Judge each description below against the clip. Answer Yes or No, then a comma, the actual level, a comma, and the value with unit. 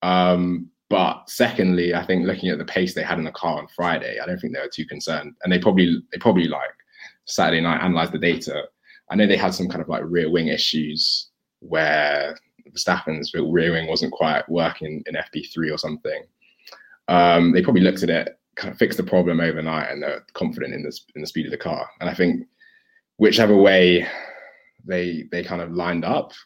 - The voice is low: Yes, very low, 90 Hz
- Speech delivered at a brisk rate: Yes, fast, 210 wpm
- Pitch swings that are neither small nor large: No, narrow, 1.9 semitones